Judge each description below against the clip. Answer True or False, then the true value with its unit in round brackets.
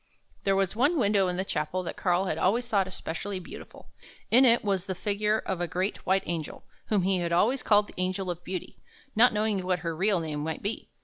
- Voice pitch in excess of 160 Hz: True (190 Hz)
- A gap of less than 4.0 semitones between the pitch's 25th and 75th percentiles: True (2.8 semitones)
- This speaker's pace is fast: True (220 wpm)